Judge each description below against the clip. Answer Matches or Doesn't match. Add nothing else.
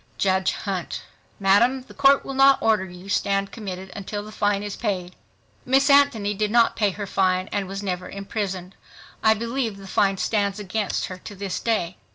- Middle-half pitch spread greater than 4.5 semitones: Doesn't match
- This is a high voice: Matches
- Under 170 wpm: Doesn't match